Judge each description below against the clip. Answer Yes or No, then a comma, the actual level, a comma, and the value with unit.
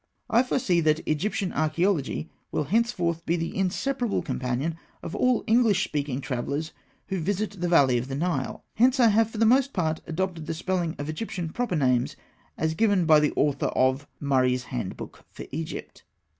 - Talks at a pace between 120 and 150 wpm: No, average, 170 wpm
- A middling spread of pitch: No, wide, 5.9 semitones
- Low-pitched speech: No, medium, 165 Hz